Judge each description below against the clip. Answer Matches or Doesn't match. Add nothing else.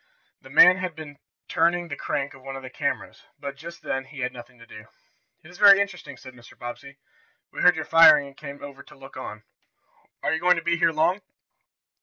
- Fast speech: Matches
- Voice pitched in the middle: Matches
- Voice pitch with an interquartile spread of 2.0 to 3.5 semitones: Doesn't match